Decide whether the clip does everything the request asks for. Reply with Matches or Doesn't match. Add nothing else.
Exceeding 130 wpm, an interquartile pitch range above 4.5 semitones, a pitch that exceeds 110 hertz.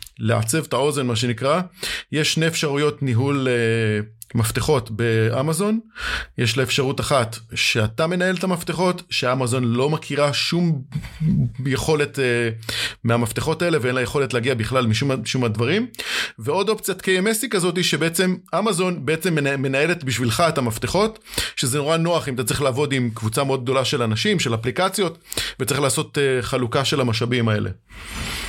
Matches